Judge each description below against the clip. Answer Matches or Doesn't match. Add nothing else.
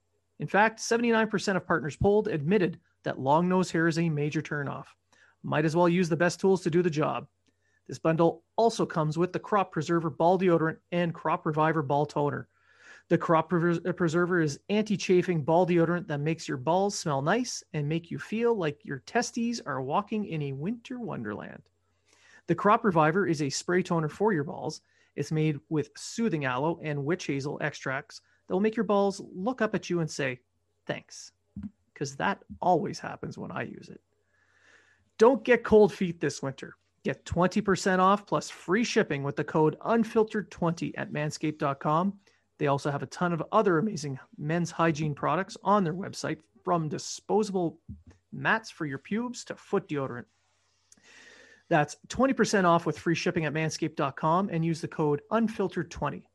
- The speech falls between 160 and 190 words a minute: Matches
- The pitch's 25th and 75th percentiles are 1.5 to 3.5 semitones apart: Doesn't match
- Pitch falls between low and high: Matches